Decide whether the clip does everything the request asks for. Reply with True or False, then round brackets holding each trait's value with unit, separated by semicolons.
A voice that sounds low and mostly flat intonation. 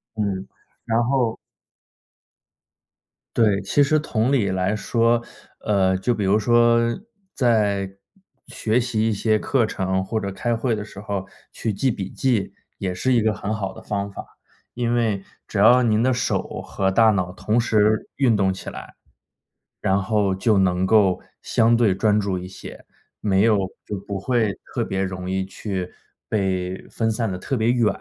False (105 Hz; 3.2 semitones)